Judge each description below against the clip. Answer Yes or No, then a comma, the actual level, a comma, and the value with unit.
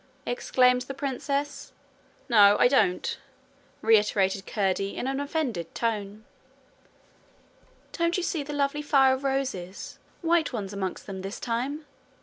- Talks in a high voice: Yes, very high, 250 Hz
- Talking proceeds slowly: Yes, slow, 130 wpm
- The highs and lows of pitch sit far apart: Yes, wide, 5.8 semitones